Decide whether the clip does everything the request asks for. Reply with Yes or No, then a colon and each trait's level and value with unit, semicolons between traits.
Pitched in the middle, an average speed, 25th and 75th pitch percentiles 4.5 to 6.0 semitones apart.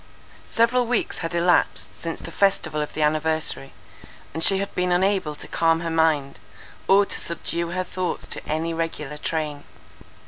No: medium, 165 Hz; average, 165 wpm; average, 3.0 semitones